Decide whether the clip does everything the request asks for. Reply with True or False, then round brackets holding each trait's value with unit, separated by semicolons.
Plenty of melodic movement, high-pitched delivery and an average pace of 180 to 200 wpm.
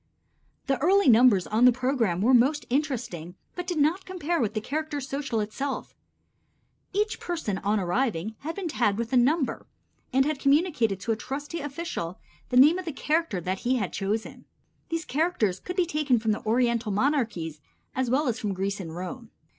True (6.1 semitones; 255 Hz; 185 wpm)